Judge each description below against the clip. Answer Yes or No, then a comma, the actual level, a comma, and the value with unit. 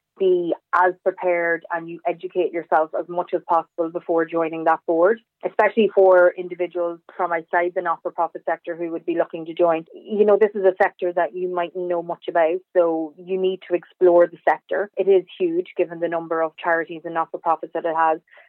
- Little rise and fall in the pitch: Yes, narrow, 1.7 semitones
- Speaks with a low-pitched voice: No, medium, 175 Hz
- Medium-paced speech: No, fast, 215 wpm